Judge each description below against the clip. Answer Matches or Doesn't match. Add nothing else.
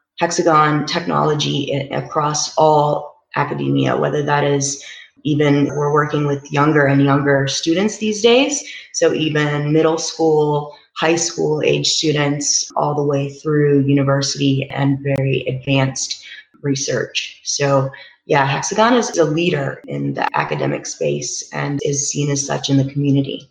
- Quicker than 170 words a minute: Doesn't match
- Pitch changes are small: Matches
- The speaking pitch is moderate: Matches